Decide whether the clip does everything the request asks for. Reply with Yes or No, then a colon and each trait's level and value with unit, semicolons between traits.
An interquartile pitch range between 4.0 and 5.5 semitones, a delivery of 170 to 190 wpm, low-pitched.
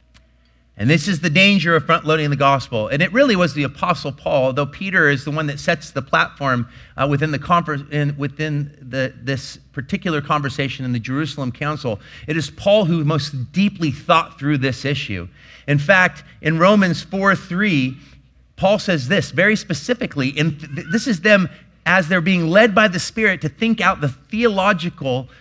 No: average, 5.1 semitones; average, 180 wpm; medium, 155 Hz